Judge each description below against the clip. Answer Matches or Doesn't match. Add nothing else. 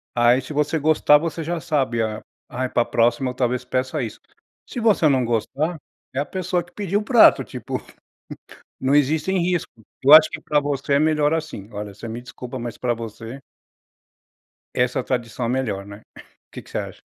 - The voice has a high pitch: Doesn't match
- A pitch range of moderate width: Matches